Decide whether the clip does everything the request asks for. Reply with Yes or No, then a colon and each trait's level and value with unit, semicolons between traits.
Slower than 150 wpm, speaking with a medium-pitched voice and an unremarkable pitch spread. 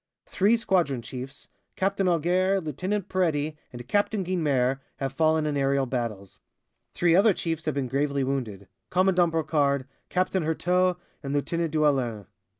Yes: average, 140 wpm; medium, 155 Hz; average, 5.0 semitones